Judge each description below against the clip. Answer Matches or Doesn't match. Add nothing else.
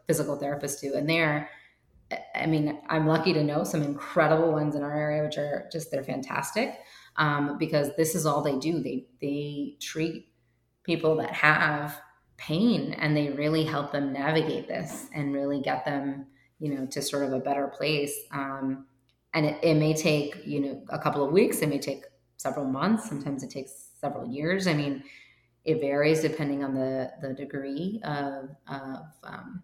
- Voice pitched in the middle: Matches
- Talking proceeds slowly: Doesn't match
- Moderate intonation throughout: Doesn't match